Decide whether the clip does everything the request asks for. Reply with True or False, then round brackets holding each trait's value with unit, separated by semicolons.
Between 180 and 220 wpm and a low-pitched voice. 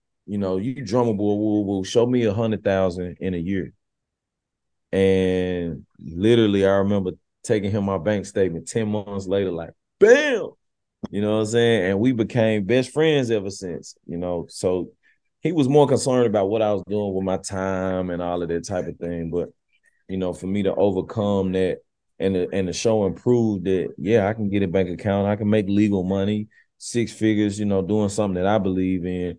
True (200 wpm; 100 Hz)